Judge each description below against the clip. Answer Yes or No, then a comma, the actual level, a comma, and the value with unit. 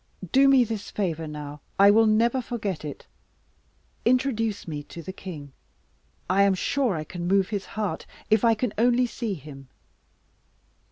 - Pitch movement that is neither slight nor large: No, wide, 5.8 semitones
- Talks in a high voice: Yes, high, 200 Hz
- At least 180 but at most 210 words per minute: No, average, 160 wpm